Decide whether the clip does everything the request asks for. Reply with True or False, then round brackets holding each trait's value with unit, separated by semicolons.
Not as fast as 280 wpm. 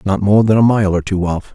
False (310 wpm)